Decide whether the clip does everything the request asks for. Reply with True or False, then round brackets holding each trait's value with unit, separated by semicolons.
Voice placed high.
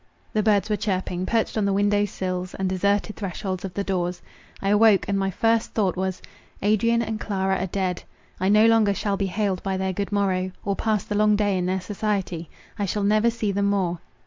True (200 Hz)